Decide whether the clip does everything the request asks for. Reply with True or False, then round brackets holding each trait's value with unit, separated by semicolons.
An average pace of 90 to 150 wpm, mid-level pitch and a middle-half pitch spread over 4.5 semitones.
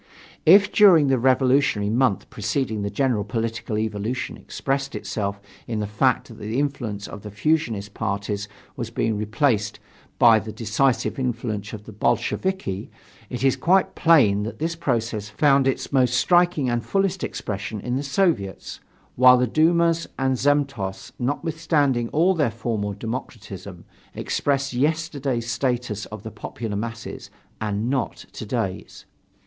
False (145 wpm; 120 Hz; 4.9 semitones)